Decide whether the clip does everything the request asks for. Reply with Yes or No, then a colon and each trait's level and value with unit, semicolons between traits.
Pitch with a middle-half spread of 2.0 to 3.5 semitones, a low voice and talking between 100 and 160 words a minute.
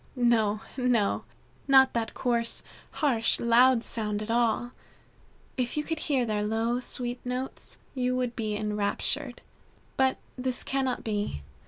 No: narrow, 2.5 semitones; high, 240 Hz; slow, 135 wpm